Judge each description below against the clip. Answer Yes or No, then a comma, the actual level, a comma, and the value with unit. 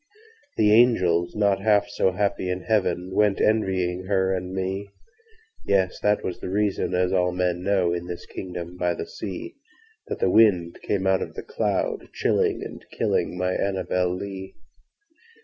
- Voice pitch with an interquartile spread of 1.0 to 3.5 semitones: Yes, narrow, 2.4 semitones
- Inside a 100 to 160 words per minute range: Yes, average, 150 wpm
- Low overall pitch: Yes, very low, 95 Hz